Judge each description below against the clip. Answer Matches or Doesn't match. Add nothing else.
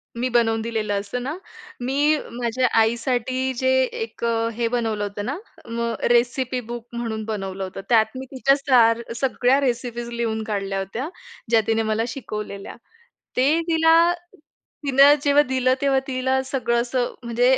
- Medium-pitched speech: Doesn't match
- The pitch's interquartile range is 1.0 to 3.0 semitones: Matches